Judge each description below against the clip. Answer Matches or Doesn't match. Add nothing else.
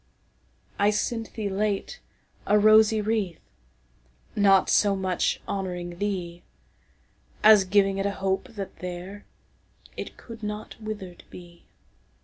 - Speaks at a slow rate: Matches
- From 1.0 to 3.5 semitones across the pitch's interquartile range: Matches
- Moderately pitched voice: Doesn't match